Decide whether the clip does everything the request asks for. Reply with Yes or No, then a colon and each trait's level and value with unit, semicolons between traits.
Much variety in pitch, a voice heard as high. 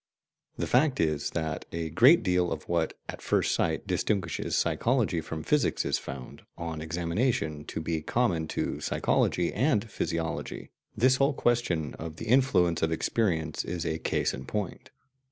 No: wide, 6.4 semitones; very low, 85 Hz